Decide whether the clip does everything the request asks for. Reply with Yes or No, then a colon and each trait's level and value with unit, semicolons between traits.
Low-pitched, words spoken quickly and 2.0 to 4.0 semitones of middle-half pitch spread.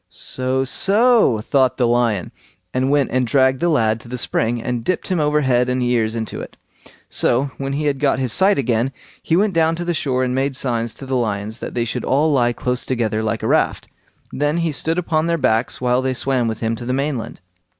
Yes: low, 130 Hz; fast, 225 wpm; average, 3.6 semitones